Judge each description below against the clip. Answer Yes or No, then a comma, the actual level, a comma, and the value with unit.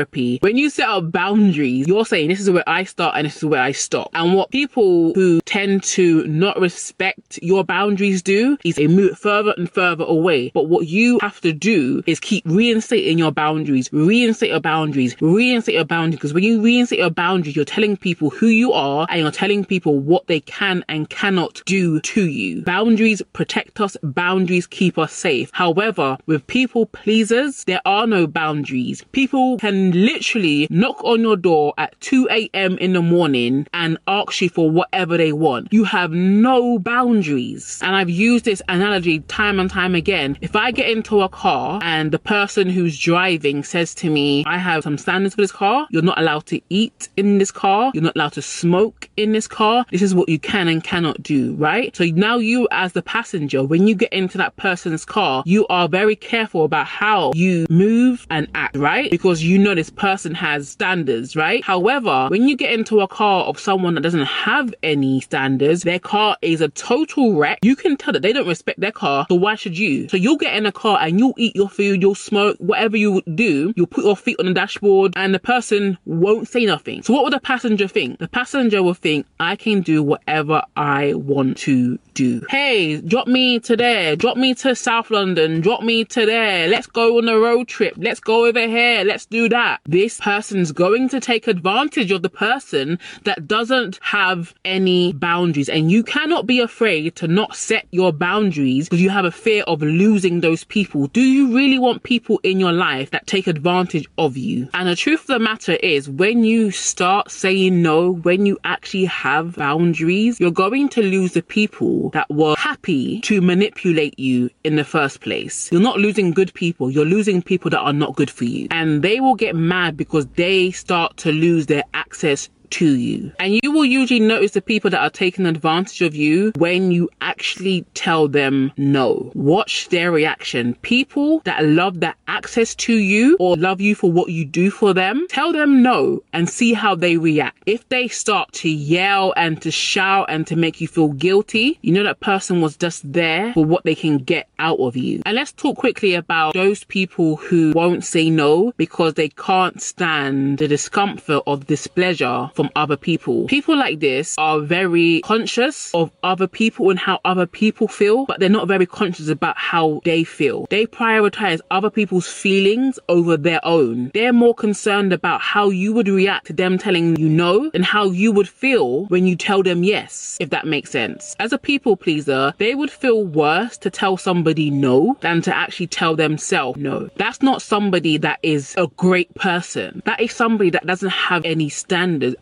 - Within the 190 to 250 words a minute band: Yes, average, 200 wpm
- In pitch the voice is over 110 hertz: Yes, medium, 185 Hz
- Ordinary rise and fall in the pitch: Yes, average, 4.9 semitones